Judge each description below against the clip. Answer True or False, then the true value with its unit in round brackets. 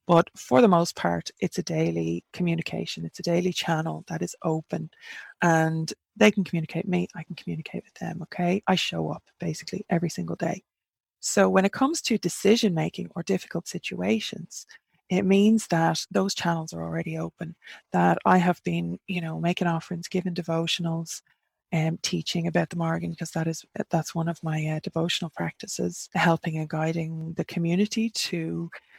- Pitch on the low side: False (170 Hz)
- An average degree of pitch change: False (2.2 semitones)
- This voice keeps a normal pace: True (175 wpm)